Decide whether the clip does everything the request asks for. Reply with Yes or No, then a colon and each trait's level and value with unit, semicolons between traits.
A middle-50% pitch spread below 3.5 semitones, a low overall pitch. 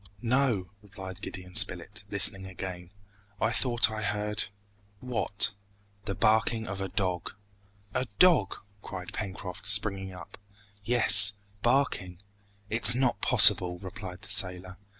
Yes: average, 2.9 semitones; low, 100 Hz